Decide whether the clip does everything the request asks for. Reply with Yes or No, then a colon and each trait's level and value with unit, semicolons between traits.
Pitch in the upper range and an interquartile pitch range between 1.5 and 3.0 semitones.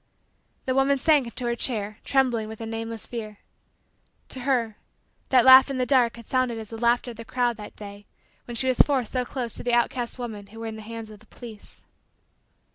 Yes: high, 235 Hz; narrow, 2.5 semitones